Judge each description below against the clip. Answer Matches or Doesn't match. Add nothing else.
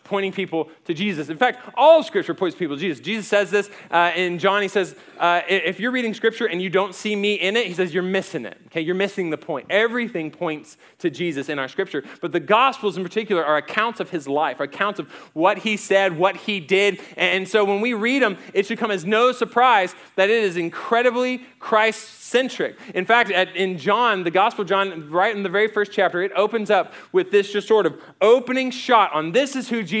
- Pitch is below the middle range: Doesn't match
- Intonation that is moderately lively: Matches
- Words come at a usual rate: Doesn't match